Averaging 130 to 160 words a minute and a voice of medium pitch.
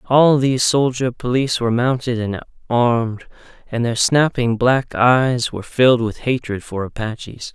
No: average, 150 wpm; low, 120 Hz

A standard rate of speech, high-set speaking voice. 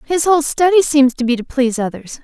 No: fast, 240 wpm; very high, 280 Hz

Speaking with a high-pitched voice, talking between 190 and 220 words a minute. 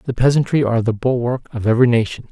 No: low, 120 Hz; fast, 205 wpm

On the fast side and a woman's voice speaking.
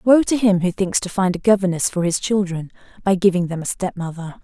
Yes: fast, 230 wpm; female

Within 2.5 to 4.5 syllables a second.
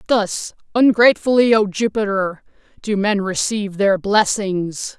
Yes: 4.3 syllables/s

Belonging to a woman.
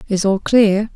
Yes: female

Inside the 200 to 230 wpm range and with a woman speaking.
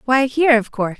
No: fast, 240 wpm; female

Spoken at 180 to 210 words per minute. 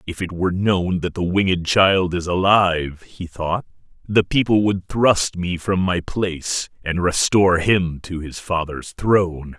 No: average, 170 wpm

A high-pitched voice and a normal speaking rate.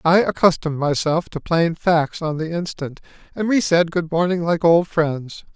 No: medium, 165 Hz; average, 185 wpm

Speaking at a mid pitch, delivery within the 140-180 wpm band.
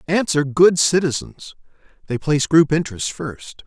Yes: medium, 155 Hz; average, 145 wpm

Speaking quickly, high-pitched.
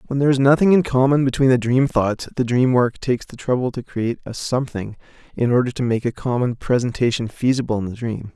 No: fast, 225 wpm; low, 125 Hz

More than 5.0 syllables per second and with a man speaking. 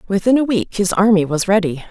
No: 6.0 syllables/s; female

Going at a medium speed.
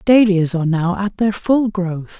Yes: average, 190 wpm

